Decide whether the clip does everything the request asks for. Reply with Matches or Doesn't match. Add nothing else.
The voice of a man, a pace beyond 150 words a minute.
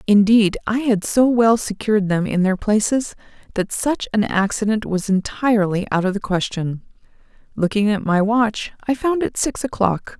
Doesn't match